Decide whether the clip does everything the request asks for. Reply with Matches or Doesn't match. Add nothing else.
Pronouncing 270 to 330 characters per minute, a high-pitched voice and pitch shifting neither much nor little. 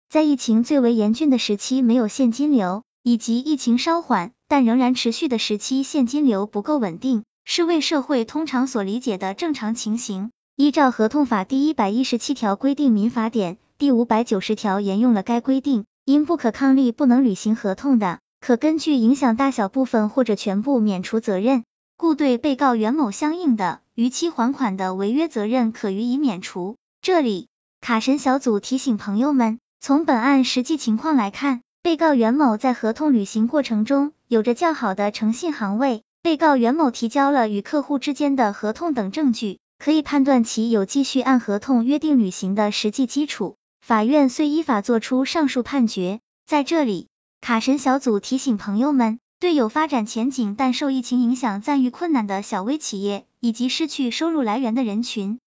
Matches